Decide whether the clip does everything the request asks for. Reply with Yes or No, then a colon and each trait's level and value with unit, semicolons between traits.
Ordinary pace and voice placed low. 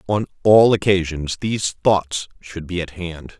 Yes: average, 160 wpm; very low, 90 Hz